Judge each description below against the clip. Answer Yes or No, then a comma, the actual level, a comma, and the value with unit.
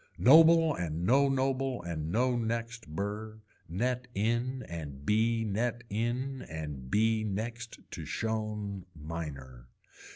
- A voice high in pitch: No, low, 110 Hz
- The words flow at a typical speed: No, slow, 120 wpm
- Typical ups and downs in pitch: No, wide, 6.1 semitones